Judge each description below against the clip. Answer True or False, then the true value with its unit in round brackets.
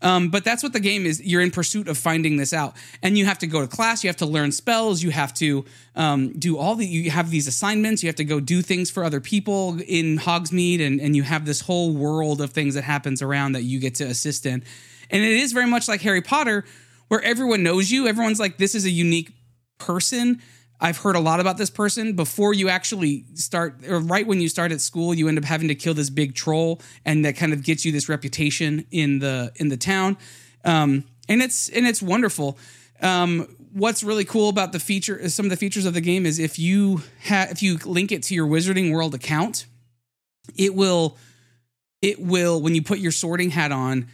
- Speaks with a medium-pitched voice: True (170 Hz)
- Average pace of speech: False (230 wpm)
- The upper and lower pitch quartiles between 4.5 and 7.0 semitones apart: True (5.0 semitones)